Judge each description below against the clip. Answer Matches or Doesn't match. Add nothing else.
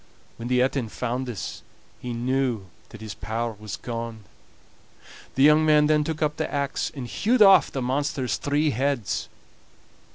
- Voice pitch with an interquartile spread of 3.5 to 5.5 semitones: Matches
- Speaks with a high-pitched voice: Doesn't match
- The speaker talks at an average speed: Matches